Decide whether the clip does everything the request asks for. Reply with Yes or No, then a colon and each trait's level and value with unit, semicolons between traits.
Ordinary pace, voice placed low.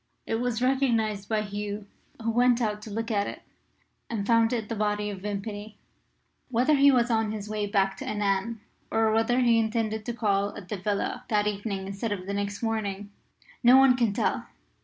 No: average, 190 wpm; high, 215 Hz